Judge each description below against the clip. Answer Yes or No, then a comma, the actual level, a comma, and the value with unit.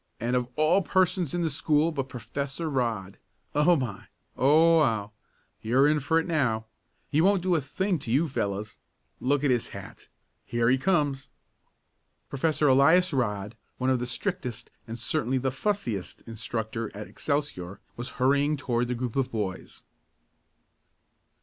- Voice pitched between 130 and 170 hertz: Yes, low, 135 Hz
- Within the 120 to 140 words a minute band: No, average, 155 wpm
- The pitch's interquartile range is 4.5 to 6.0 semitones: Yes, average, 4.8 semitones